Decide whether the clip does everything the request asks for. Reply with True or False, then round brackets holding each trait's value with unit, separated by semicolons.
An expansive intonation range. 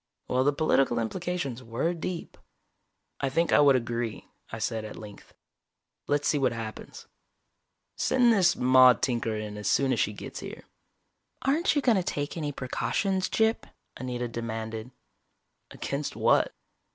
True (6.5 semitones)